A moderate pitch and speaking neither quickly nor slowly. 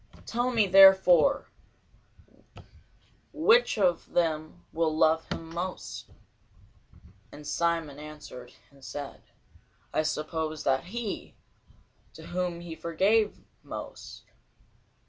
No: medium, 170 Hz; slow, 90 wpm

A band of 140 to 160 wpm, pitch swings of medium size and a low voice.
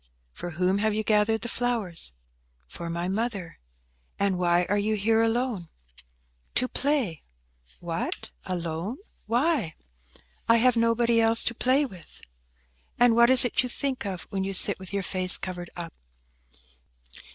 No: average, 150 wpm; average, 4.6 semitones; high, 215 Hz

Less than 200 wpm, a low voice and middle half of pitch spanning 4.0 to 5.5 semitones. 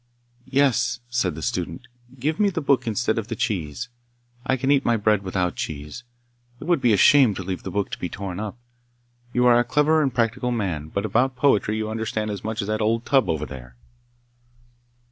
No: fast, 205 wpm; low, 115 Hz; average, 4.4 semitones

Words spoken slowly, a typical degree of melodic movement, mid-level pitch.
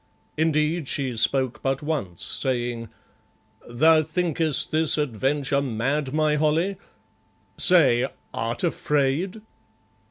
Yes: slow, 95 wpm; average, 3.4 semitones; medium, 145 Hz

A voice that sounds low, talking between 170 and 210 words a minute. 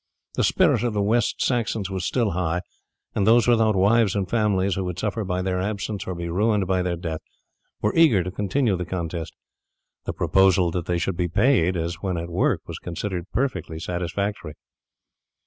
Yes: very low, 95 Hz; average, 185 wpm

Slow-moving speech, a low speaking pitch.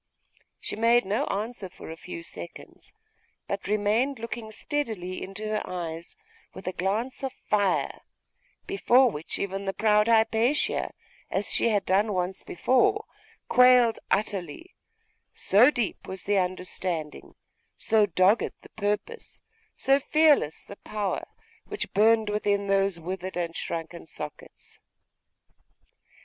No: slow, 125 wpm; high, 205 Hz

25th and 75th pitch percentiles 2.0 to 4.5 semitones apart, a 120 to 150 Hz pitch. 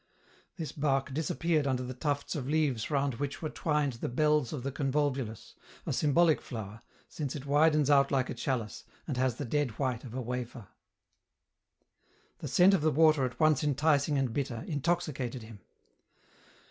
Yes: average, 3.1 semitones; medium, 140 Hz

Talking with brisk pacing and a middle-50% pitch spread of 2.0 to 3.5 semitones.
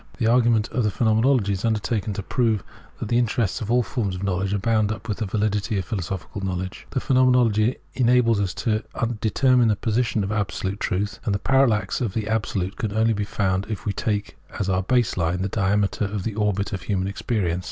Yes: fast, 215 wpm; average, 2.7 semitones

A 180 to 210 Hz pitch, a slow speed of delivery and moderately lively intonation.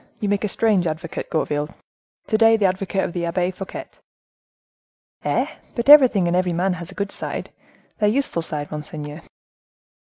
No: medium, 185 Hz; average, 155 wpm; average, 3.7 semitones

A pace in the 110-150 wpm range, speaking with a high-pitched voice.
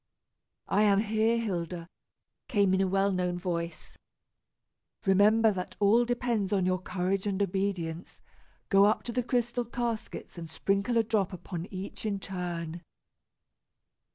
Yes: average, 140 wpm; high, 195 Hz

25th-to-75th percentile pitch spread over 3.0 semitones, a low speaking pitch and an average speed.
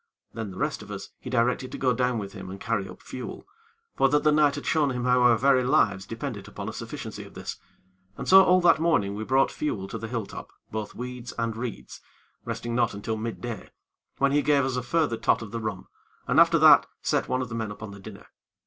No: average, 3.7 semitones; low, 120 Hz; fast, 240 wpm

